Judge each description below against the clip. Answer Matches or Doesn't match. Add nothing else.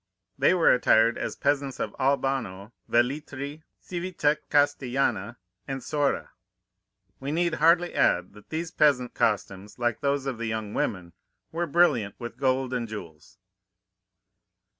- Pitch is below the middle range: Matches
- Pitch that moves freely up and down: Doesn't match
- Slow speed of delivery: Matches